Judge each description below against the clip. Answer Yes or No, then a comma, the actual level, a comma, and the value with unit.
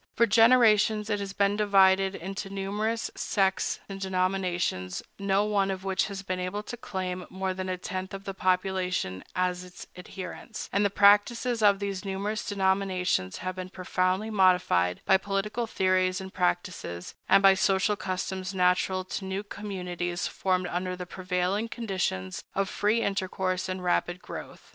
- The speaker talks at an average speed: Yes, average, 160 wpm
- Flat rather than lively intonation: Yes, narrow, 1.6 semitones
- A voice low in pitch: No, high, 190 Hz